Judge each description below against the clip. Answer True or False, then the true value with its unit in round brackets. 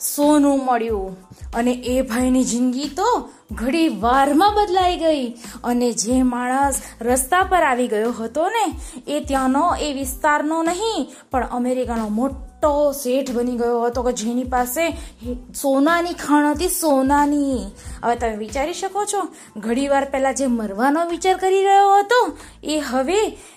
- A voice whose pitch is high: True (275 Hz)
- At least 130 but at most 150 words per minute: True (135 wpm)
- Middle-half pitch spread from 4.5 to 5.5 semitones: True (4.9 semitones)